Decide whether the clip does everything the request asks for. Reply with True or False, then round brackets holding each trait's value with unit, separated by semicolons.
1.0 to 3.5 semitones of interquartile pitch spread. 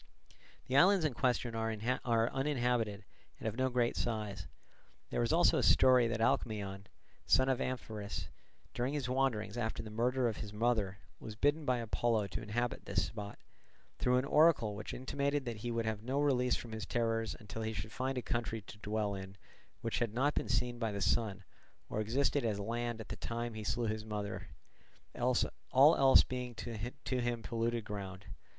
True (2.8 semitones)